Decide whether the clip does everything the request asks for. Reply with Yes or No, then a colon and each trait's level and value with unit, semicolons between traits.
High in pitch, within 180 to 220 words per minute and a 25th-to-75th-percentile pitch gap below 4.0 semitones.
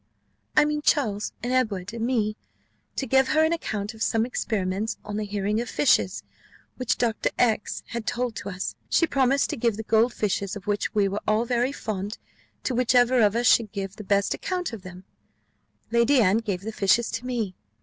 Yes: high, 225 Hz; average, 200 wpm; average, 3.3 semitones